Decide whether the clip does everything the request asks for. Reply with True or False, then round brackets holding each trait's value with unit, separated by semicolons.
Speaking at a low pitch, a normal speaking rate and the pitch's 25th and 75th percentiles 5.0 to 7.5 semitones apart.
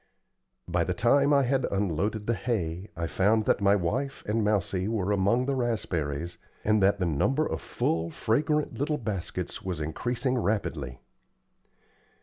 True (105 Hz; 150 wpm; 5.6 semitones)